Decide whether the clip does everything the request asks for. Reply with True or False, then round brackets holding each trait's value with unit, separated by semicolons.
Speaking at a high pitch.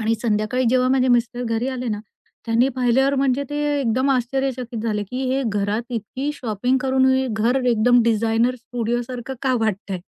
True (245 Hz)